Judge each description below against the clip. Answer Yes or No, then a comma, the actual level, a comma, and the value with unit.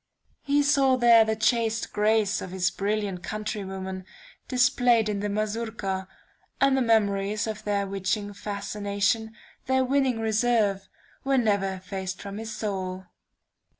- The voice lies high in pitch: Yes, high, 215 Hz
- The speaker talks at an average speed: No, slow, 130 wpm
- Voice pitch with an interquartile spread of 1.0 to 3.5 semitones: Yes, average, 2.7 semitones